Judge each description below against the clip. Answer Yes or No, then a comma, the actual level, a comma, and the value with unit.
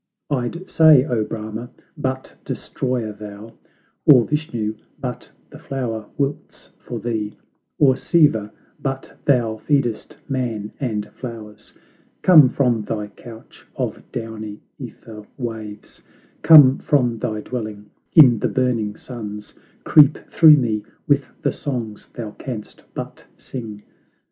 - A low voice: Yes, low, 120 Hz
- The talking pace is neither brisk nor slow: No, slow, 120 wpm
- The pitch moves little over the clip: No, average, 3.7 semitones